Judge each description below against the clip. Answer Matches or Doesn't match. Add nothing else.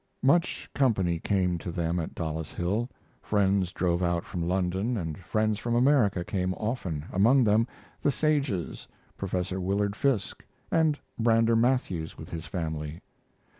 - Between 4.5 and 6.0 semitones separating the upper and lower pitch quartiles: Matches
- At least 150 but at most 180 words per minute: Doesn't match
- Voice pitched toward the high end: Doesn't match